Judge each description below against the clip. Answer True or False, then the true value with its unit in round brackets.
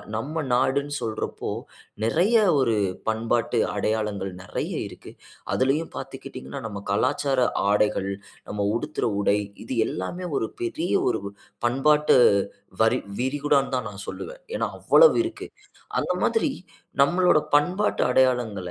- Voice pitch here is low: True (130 Hz)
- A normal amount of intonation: False (5.7 semitones)